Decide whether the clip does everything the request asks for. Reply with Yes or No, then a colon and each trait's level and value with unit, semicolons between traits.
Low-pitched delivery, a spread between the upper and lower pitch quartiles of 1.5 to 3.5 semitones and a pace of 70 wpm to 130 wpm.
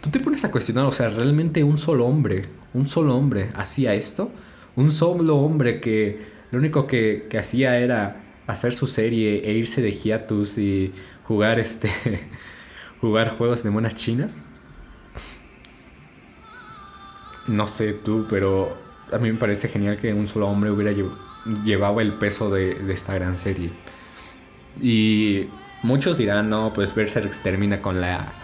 No: low, 110 Hz; average, 3.2 semitones; average, 155 wpm